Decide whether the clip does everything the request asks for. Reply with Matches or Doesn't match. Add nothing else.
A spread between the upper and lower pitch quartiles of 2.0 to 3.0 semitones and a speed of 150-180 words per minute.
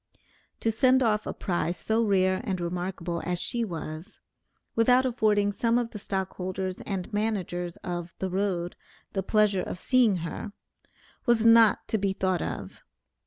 Doesn't match